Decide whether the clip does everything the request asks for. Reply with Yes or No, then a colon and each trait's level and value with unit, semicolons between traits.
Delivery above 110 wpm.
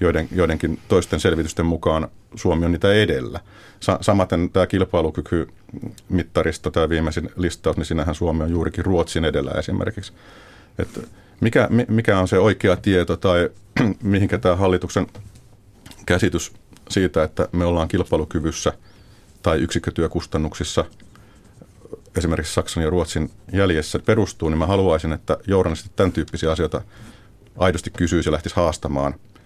Yes: average, 130 wpm